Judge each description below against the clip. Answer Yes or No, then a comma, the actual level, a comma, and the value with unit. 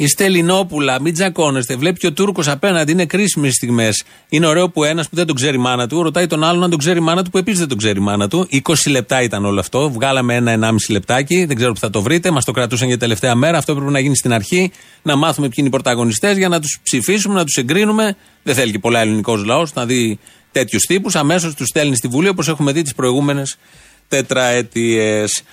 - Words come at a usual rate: No, fast, 230 wpm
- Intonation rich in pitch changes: Yes, wide, 5.7 semitones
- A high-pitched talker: No, medium, 140 Hz